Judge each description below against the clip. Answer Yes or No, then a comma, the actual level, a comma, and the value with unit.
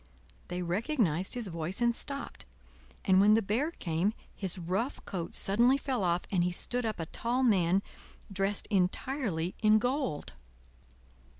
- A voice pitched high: Yes, high, 200 Hz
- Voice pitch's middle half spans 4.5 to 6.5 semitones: Yes, average, 5.1 semitones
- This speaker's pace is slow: No, average, 145 wpm